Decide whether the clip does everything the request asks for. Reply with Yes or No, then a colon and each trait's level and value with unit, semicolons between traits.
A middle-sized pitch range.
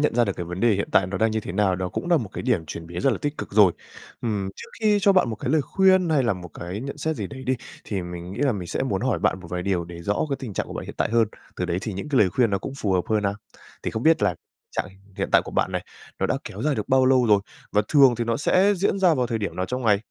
No: wide, 6.4 semitones